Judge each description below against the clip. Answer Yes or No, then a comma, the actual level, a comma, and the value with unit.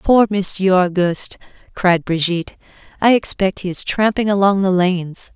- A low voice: No, high, 190 Hz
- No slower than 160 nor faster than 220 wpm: No, average, 145 wpm